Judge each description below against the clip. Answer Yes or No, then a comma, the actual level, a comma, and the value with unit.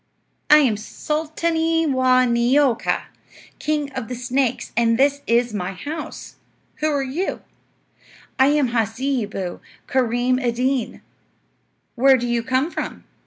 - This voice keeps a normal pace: No, slow, 125 wpm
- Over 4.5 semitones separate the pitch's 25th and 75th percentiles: No, average, 3.5 semitones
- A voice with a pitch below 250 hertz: No, very high, 255 Hz